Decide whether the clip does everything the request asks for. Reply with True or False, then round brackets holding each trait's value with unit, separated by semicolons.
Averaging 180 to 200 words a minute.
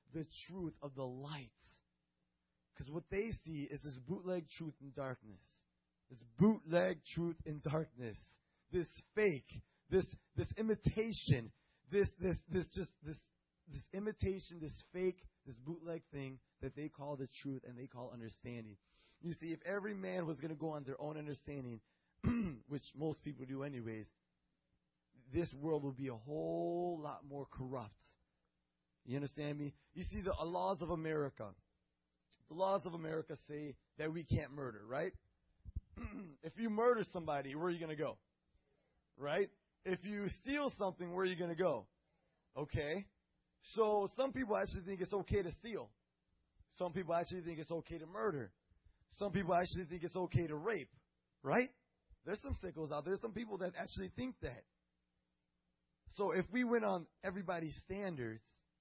False (160 wpm)